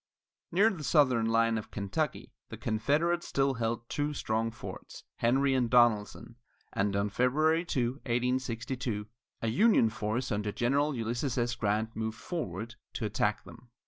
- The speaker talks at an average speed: Yes, average, 145 wpm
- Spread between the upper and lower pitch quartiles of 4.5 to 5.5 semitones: No, average, 3.7 semitones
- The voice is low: Yes, low, 120 Hz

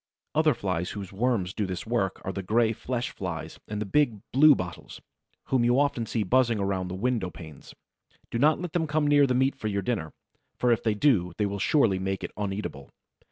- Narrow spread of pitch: No, average, 5.2 semitones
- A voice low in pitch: Yes, low, 110 Hz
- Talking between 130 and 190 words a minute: No, fast, 205 wpm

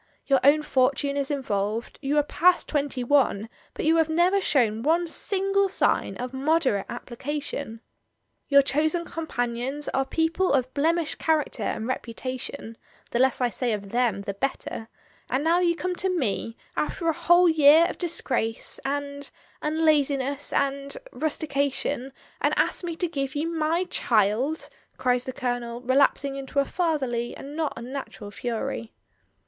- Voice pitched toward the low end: No, very high, 280 Hz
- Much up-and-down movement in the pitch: No, average, 4.3 semitones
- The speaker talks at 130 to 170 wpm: Yes, average, 165 wpm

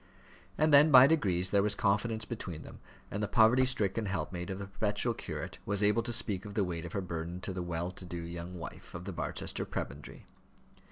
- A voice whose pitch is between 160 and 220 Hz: No, low, 100 Hz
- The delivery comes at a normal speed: No, fast, 215 wpm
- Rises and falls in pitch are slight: No, average, 3.9 semitones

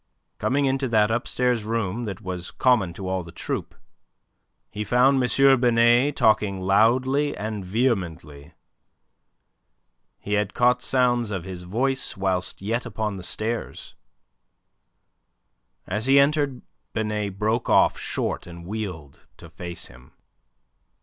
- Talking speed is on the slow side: Yes, slow, 125 wpm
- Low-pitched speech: Yes, low, 110 Hz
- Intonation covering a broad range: No, average, 4.7 semitones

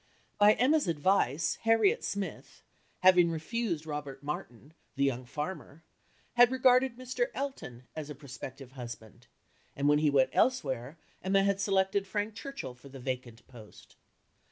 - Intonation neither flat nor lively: No, wide, 7.5 semitones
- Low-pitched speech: No, medium, 155 Hz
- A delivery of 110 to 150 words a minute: Yes, average, 140 wpm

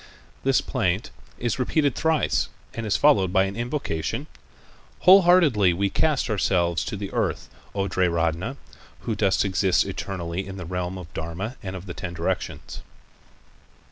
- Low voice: Yes, very low, 95 Hz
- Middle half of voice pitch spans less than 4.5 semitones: No, average, 4.9 semitones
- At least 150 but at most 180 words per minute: No, average, 140 wpm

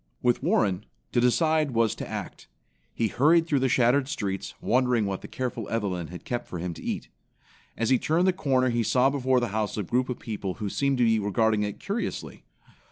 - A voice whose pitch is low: Yes, low, 120 Hz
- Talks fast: Yes, fast, 210 wpm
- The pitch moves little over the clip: No, average, 4.0 semitones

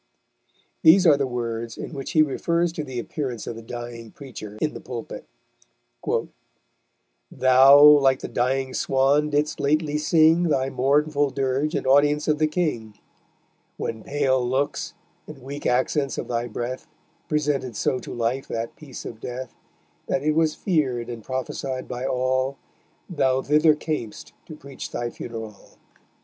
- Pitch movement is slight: No, average, 3.6 semitones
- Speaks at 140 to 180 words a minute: Yes, average, 150 wpm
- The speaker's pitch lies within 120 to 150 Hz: Yes, low, 135 Hz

